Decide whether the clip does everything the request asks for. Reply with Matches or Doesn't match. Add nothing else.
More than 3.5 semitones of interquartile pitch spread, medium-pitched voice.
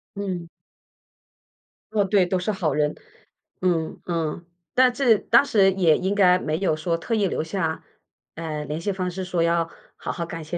Doesn't match